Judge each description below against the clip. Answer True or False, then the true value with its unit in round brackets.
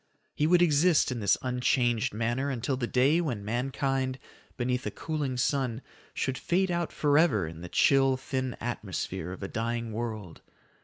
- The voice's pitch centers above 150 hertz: False (125 Hz)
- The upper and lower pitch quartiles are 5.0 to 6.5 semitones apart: False (3.6 semitones)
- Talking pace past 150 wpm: True (160 wpm)